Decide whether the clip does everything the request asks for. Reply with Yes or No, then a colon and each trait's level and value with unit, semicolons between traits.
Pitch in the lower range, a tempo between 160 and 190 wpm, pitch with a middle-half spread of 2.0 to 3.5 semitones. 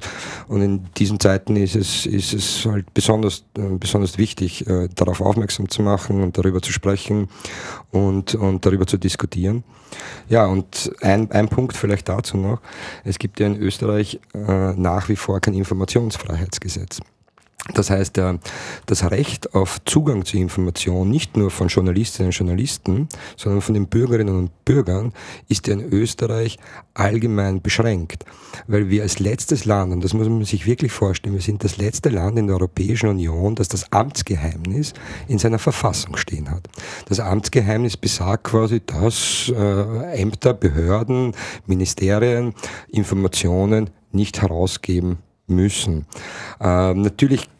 No: low, 100 Hz; average, 140 wpm; narrow, 2.6 semitones